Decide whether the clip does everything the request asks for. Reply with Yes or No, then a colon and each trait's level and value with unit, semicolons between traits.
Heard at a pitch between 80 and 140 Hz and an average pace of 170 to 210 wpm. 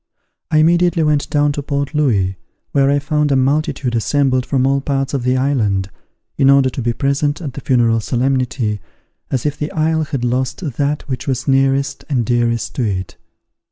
Yes: low, 135 Hz; average, 185 wpm